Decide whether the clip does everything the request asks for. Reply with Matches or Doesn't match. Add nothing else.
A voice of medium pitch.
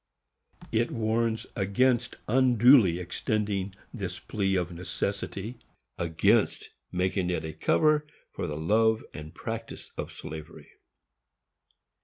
Doesn't match